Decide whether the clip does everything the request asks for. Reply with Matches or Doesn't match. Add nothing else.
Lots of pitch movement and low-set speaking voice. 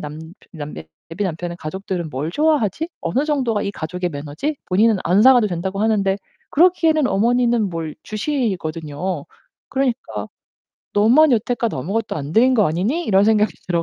Doesn't match